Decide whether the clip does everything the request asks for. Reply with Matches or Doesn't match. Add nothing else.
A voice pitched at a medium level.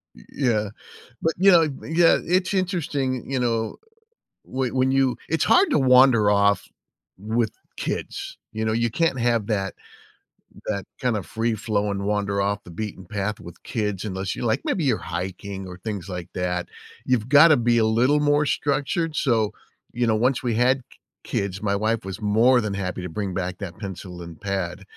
Doesn't match